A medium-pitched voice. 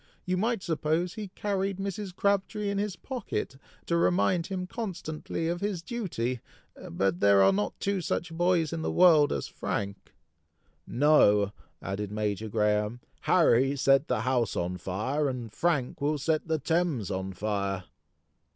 Yes: medium, 155 Hz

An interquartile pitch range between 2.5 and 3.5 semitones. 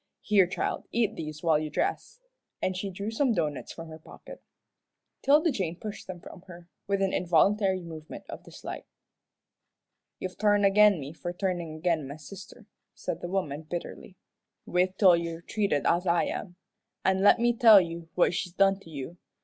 Yes: average, 3.2 semitones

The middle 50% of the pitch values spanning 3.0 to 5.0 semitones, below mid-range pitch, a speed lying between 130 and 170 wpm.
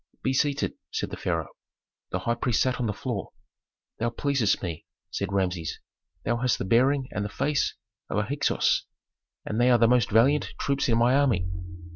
No: average, 4.1 semitones; low, 120 Hz; average, 185 wpm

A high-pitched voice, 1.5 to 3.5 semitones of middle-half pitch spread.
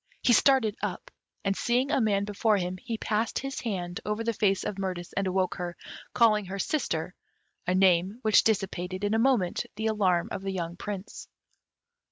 Yes: high, 200 Hz; average, 3.2 semitones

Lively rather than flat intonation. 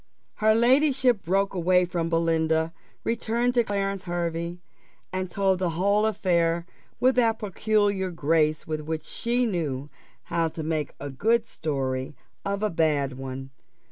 No: average, 4.7 semitones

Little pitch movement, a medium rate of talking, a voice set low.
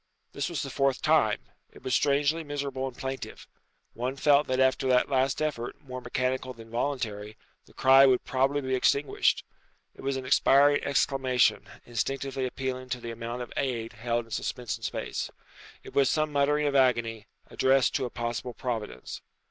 Yes: narrow, 2.2 semitones; average, 170 wpm; low, 130 Hz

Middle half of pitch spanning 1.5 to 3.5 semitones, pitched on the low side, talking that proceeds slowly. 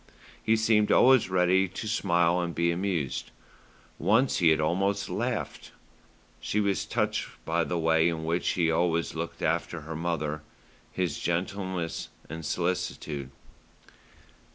Yes: average, 2.8 semitones; very low, 85 Hz; slow, 130 wpm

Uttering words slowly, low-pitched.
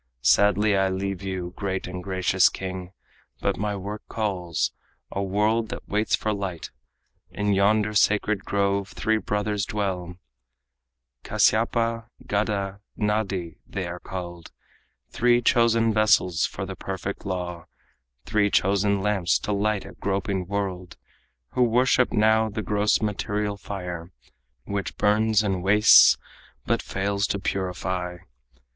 Yes: slow, 125 wpm; low, 100 Hz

